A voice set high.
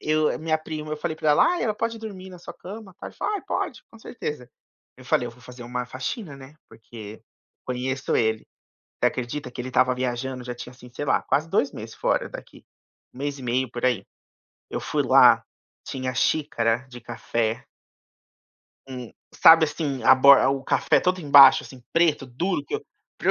No: low, 135 Hz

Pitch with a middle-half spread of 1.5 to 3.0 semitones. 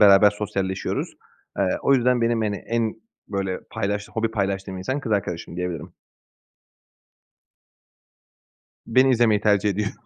Yes: average, 2.7 semitones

